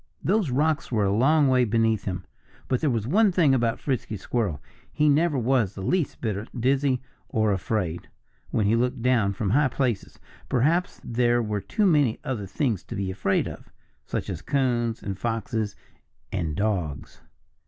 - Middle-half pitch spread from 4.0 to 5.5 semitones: Yes, average, 4.7 semitones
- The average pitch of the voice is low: Yes, low, 120 Hz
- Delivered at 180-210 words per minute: No, average, 170 wpm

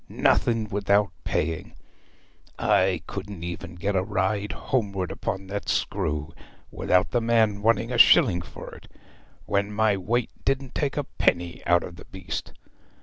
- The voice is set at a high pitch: No, low, 100 Hz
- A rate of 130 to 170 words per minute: Yes, average, 145 wpm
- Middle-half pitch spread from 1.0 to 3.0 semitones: No, average, 3.8 semitones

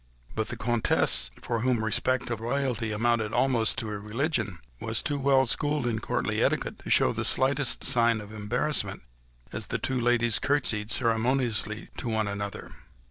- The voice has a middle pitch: No, low, 115 Hz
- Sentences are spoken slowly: No, average, 165 wpm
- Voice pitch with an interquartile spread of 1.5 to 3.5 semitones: Yes, average, 3.0 semitones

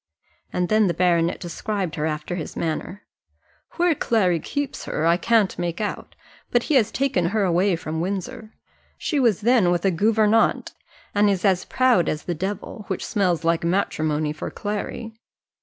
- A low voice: No, high, 190 Hz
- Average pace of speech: Yes, average, 175 wpm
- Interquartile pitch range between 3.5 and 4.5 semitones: Yes, average, 4.2 semitones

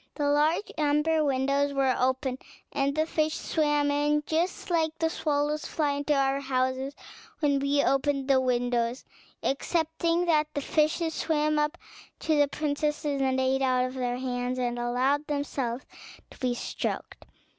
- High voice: Yes, very high, 285 Hz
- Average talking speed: Yes, average, 150 wpm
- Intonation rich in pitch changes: No, narrow, 2.5 semitones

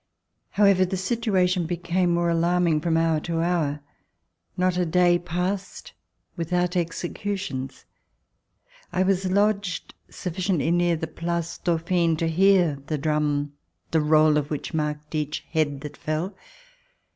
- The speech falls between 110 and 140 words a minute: Yes, slow, 135 wpm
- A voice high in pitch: No, medium, 170 Hz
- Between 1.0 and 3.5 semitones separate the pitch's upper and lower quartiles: Yes, average, 2.7 semitones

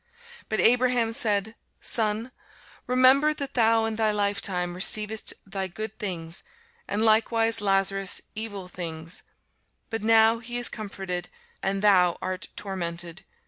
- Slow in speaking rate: Yes, slow, 125 wpm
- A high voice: Yes, high, 210 Hz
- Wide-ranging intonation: No, average, 3.1 semitones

